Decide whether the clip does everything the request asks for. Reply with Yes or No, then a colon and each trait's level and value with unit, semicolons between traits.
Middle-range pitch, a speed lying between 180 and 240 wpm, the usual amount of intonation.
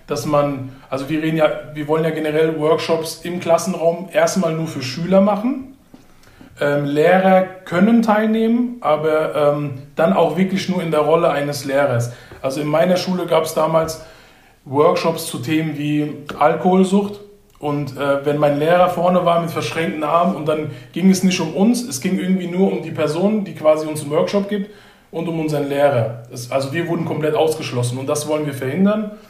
Yes: medium, 160 Hz; average, 185 wpm; average, 3.6 semitones